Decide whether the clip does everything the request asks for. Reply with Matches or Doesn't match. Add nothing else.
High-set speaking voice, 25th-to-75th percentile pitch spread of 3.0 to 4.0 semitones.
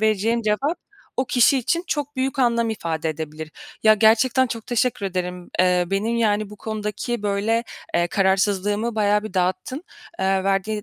Matches